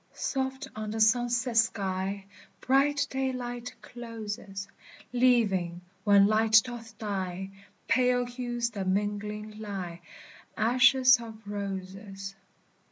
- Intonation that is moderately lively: Yes, average, 3.6 semitones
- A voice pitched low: No, high, 220 Hz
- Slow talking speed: Yes, slow, 100 wpm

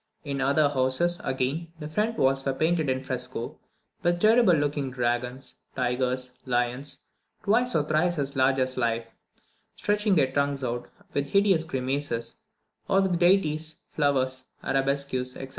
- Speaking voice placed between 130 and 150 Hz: Yes, medium, 140 Hz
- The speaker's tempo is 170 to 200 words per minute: No, average, 140 wpm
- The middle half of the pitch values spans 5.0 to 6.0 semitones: No, average, 3.9 semitones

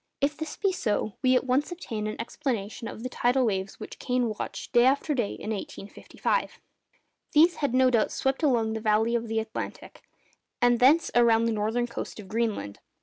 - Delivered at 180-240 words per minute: Yes, average, 190 wpm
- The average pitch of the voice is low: No, high, 240 Hz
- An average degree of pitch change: Yes, average, 3.3 semitones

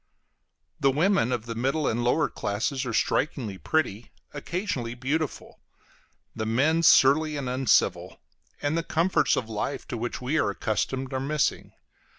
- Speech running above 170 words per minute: No, average, 150 wpm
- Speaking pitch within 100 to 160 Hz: Yes, low, 135 Hz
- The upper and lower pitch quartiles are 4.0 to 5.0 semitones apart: Yes, average, 4.6 semitones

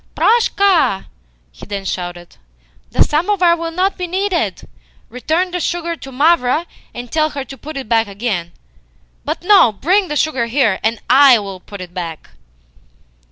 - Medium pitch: No, very high, 275 Hz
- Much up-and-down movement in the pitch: Yes, wide, 8.6 semitones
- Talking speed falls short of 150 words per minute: No, average, 160 wpm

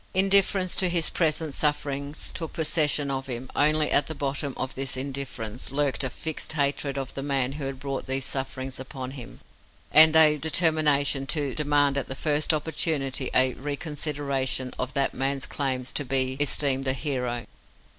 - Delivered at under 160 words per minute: No, average, 165 wpm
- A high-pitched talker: No, medium, 140 Hz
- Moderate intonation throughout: No, narrow, 2.3 semitones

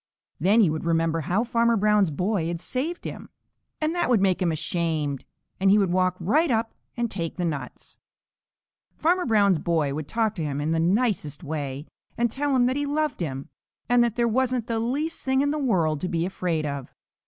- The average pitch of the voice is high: Yes, high, 195 Hz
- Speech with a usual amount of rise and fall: No, wide, 6.9 semitones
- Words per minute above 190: Yes, fast, 205 wpm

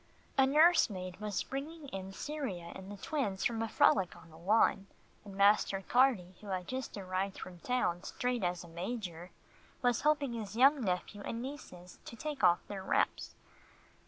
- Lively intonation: Yes, wide, 5.8 semitones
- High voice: Yes, high, 205 Hz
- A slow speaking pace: No, average, 175 wpm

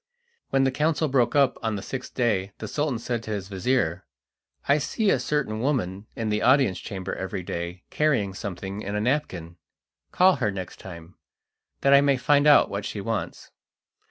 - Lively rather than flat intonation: Yes, wide, 6.2 semitones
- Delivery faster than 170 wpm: Yes, average, 185 wpm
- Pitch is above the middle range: No, low, 110 Hz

